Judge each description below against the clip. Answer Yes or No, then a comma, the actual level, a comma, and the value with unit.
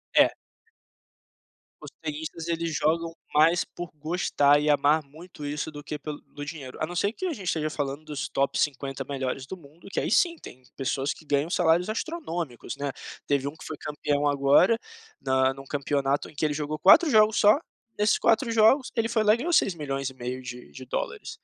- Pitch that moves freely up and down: No, average, 4.1 semitones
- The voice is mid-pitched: Yes, medium, 150 Hz